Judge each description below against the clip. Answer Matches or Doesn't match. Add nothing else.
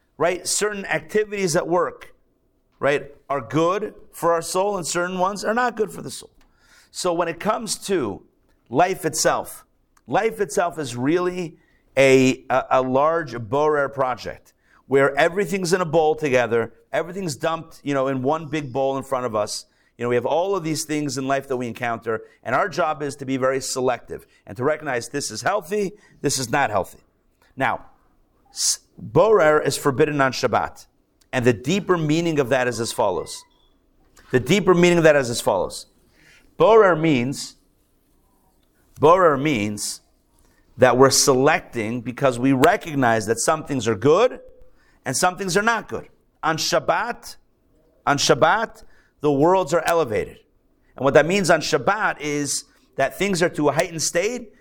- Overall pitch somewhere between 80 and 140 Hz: Doesn't match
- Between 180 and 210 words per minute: Doesn't match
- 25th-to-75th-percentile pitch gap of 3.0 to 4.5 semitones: Doesn't match